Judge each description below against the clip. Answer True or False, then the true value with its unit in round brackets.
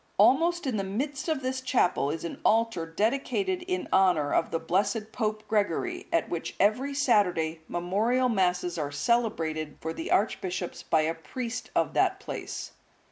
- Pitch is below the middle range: False (210 Hz)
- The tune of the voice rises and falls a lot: True (7.3 semitones)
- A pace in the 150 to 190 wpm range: True (165 wpm)